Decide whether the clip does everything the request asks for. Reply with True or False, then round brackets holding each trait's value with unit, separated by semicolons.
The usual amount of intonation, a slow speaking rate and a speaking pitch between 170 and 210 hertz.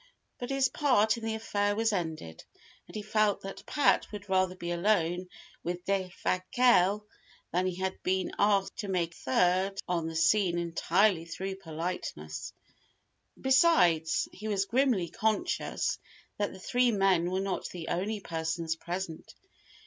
False (3.6 semitones; 150 wpm; 190 Hz)